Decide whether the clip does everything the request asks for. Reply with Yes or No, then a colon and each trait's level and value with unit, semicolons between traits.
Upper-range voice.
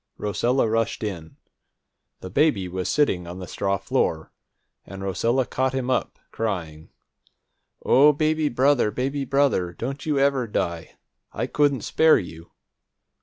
No: low, 115 Hz